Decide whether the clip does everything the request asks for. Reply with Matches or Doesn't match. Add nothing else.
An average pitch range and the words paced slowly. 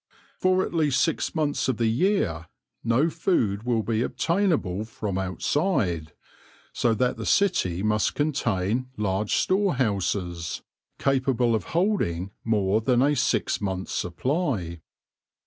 Doesn't match